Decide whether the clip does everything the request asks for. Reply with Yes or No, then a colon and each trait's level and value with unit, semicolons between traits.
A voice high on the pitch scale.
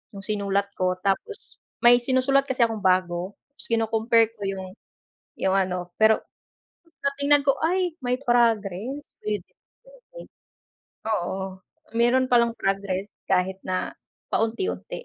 Yes: high, 220 Hz